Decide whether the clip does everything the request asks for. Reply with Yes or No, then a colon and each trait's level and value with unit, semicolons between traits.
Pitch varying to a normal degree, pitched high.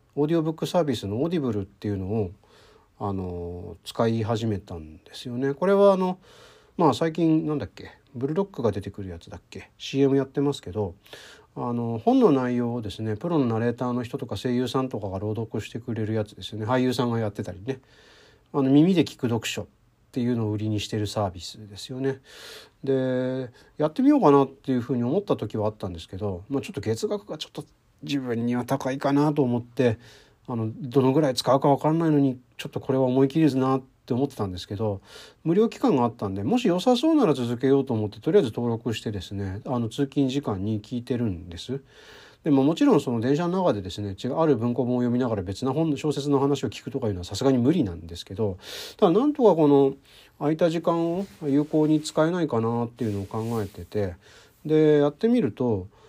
No: average, 5.0 semitones; low, 125 Hz